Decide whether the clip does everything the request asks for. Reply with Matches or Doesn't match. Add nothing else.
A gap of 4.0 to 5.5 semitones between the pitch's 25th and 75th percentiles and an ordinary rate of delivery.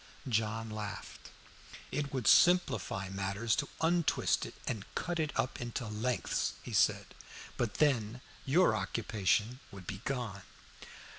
Doesn't match